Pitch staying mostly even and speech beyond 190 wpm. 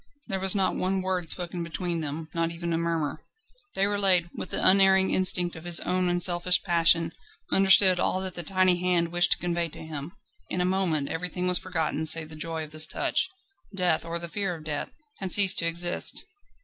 Yes: narrow, 2.0 semitones; average, 200 wpm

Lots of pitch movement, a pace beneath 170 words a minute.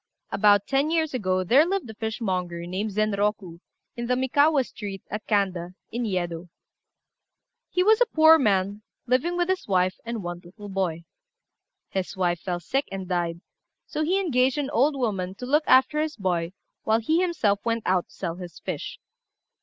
No: wide, 6.7 semitones; average, 175 wpm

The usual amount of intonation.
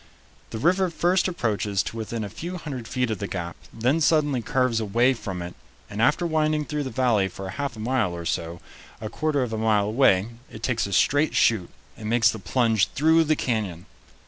No: wide, 5.8 semitones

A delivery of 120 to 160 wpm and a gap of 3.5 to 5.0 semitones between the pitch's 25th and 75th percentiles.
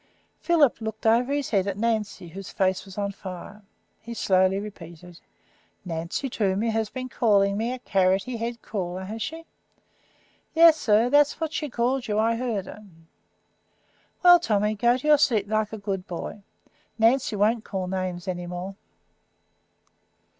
Yes: average, 155 wpm; average, 3.9 semitones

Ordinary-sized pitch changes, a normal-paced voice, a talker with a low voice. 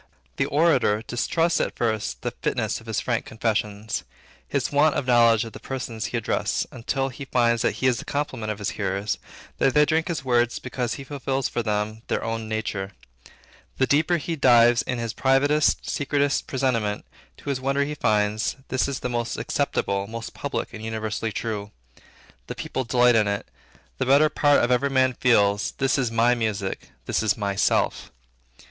Yes: average, 3.7 semitones; average, 180 wpm; low, 120 Hz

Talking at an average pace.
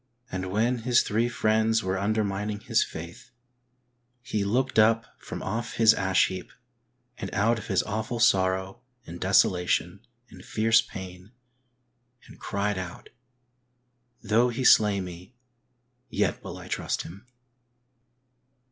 No: slow, 130 wpm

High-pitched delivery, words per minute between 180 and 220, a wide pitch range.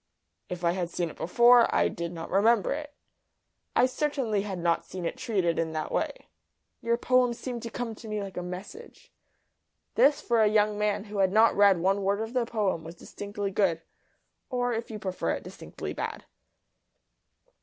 No: high, 210 Hz; average, 185 wpm; average, 4.5 semitones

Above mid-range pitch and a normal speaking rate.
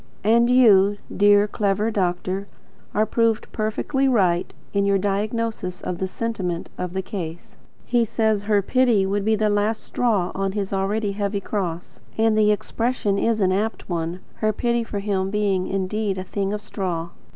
Yes: high, 205 Hz; average, 170 wpm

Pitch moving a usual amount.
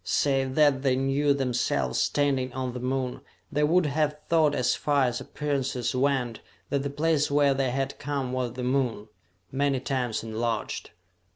No: narrow, 2.2 semitones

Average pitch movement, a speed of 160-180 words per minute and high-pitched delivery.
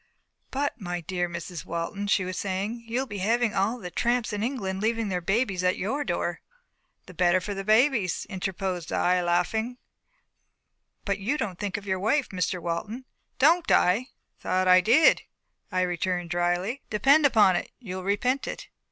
Yes: average, 4.3 semitones; average, 170 wpm; high, 195 Hz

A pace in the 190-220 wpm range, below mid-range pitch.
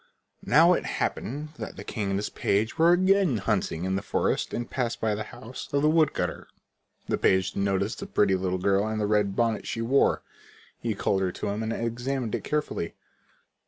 Yes: average, 200 wpm; low, 110 Hz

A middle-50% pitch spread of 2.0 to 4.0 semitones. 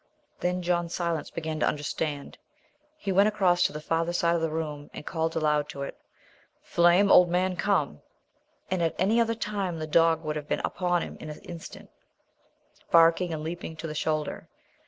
Yes: narrow, 2.5 semitones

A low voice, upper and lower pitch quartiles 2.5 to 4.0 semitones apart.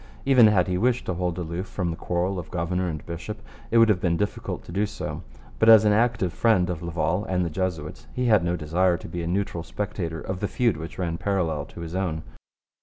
Yes: very low, 90 Hz; average, 3.4 semitones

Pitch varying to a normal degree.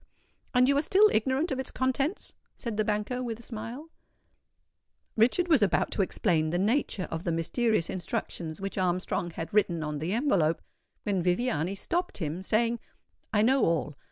No: wide, 6.5 semitones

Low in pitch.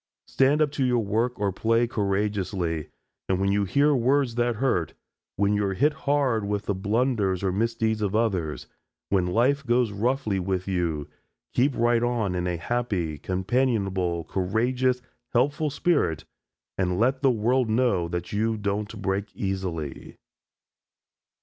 Yes: low, 105 Hz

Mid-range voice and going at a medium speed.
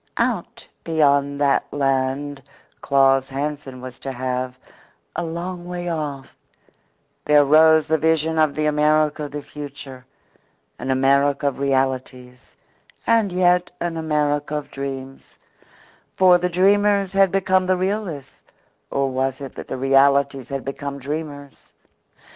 No: medium, 145 Hz; slow, 130 wpm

